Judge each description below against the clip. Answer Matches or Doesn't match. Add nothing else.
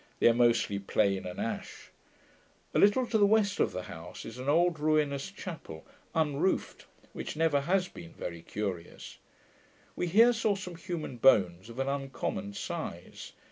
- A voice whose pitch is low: Doesn't match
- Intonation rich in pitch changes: Matches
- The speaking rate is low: Doesn't match